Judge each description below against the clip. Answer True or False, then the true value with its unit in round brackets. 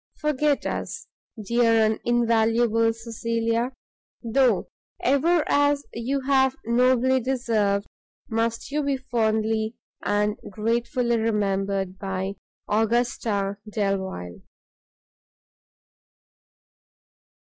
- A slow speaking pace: True (80 wpm)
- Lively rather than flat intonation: False (3.1 semitones)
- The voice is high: True (230 Hz)